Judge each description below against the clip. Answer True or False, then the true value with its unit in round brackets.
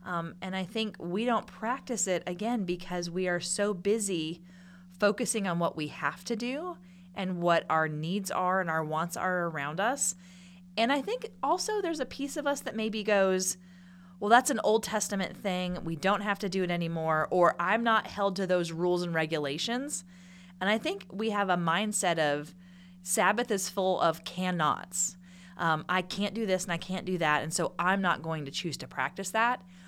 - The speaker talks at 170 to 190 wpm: False (200 wpm)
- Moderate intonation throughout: True (3.1 semitones)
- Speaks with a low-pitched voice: False (185 Hz)